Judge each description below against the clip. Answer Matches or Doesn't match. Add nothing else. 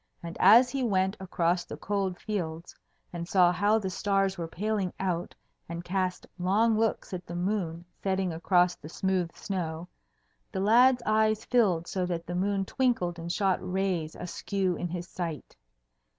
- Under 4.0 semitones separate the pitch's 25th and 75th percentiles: Matches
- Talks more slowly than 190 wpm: Matches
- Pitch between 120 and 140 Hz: Doesn't match